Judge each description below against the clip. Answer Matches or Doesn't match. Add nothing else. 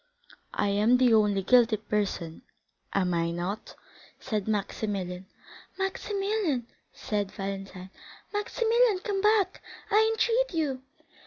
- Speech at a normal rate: Doesn't match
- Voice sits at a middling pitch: Doesn't match